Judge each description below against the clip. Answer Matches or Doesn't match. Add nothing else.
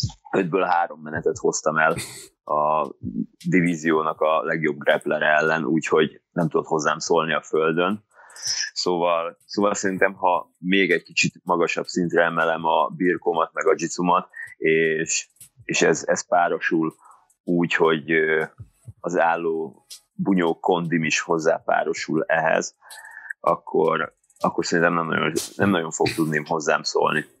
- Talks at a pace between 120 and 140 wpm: Matches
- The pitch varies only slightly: Matches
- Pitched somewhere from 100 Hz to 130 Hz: Doesn't match